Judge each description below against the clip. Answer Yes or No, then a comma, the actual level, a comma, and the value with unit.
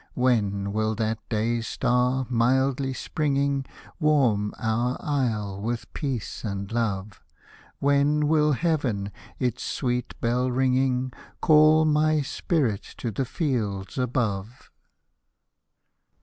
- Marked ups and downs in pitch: No, average, 4.2 semitones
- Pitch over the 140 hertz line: No, low, 125 Hz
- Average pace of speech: No, slow, 105 wpm